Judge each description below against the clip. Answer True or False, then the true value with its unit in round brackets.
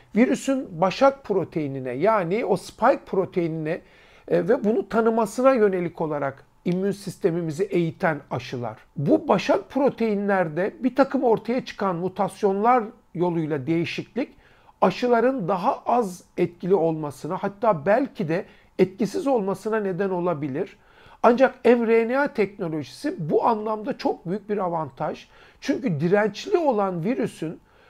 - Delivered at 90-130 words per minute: True (110 wpm)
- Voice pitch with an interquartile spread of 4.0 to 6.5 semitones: True (5.1 semitones)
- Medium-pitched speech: False (200 Hz)